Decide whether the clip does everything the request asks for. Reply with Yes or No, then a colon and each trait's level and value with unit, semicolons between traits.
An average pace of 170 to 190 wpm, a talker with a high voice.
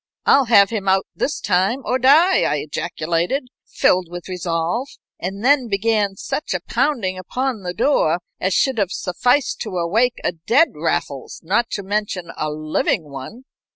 No: average, 160 wpm; high, 195 Hz